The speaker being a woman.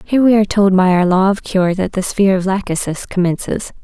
Yes: female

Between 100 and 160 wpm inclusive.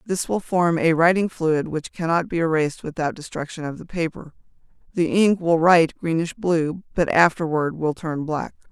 No: average, 180 wpm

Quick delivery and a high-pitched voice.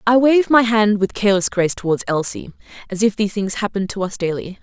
Yes: fast, 210 wpm; high, 205 Hz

